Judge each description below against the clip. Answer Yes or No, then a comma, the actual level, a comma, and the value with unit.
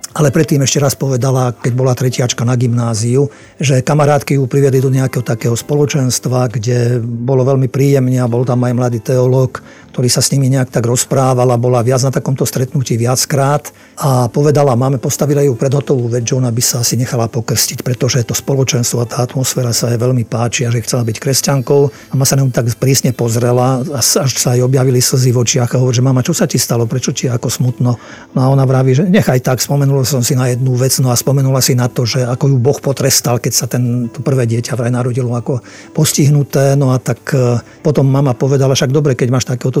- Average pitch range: No, narrow, 2.0 semitones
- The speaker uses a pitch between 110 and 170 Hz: Yes, low, 130 Hz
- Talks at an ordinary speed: No, fast, 215 wpm